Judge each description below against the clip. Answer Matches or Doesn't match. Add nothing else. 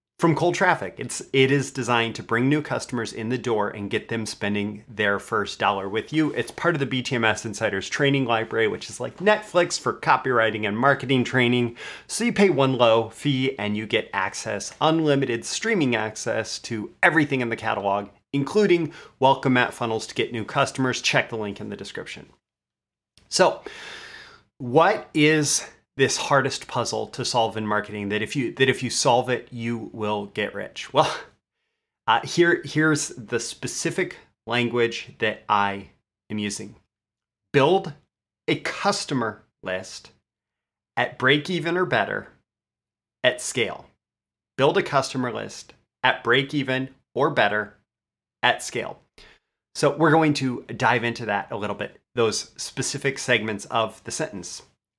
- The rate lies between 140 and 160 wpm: Matches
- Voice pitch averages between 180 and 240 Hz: Doesn't match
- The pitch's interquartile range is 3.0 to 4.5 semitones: Doesn't match